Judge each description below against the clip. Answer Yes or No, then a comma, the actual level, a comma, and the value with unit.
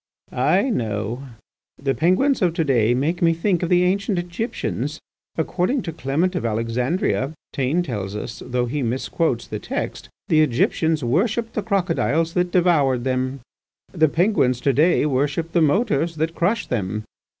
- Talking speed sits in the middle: Yes, average, 150 wpm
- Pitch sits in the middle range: Yes, medium, 160 Hz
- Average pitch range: No, wide, 5.8 semitones